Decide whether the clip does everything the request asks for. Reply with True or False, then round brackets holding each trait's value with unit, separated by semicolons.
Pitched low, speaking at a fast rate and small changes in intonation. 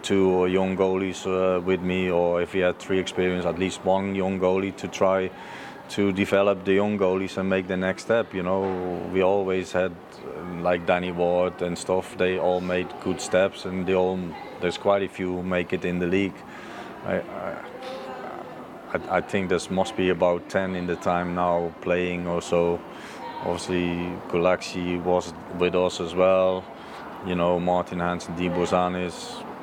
False (90 Hz; 175 wpm; 1.1 semitones)